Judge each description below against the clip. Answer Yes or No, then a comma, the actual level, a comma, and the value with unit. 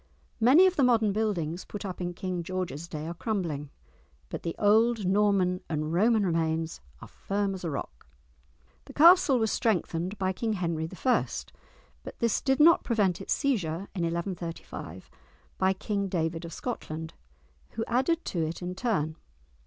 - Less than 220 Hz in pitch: Yes, medium, 185 Hz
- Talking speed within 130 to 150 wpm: No, average, 160 wpm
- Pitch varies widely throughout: No, average, 5.0 semitones